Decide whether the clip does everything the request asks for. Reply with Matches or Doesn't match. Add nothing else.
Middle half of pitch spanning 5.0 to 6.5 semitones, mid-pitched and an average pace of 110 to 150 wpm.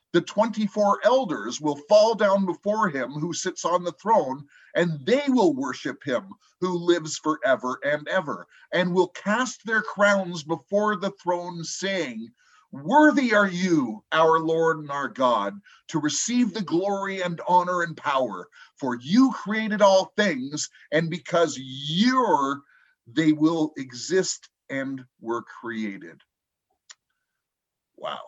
Matches